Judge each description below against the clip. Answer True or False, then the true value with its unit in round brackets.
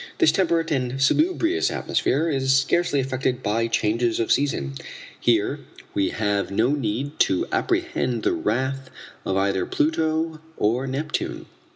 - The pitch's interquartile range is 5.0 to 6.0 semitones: True (5.3 semitones)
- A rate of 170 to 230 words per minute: False (135 wpm)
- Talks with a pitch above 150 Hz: False (130 Hz)